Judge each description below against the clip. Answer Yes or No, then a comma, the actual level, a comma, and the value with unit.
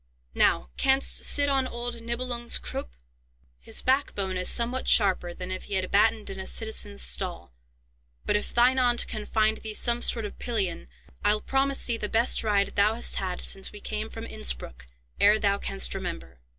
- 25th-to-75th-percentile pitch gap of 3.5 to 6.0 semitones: Yes, average, 4.1 semitones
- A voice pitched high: Yes, high, 215 Hz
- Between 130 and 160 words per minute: No, average, 185 wpm